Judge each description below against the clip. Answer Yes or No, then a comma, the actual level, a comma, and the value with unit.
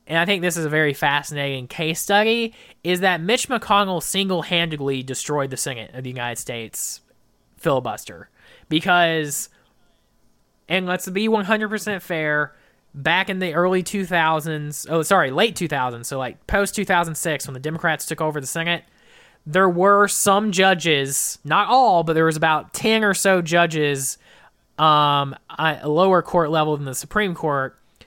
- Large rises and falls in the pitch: No, average, 4.5 semitones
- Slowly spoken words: No, average, 170 wpm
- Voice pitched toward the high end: No, medium, 165 Hz